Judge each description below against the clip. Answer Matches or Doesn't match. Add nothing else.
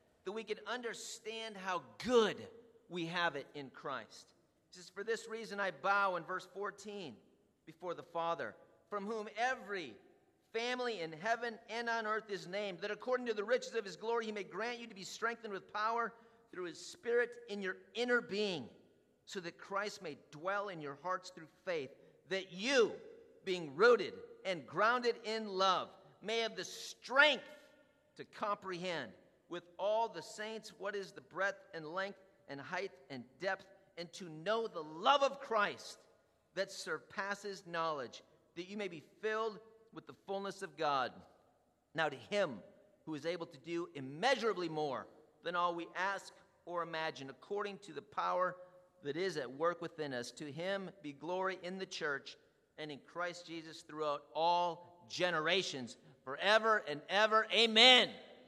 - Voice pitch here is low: Doesn't match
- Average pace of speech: Matches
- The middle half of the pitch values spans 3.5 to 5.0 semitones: Matches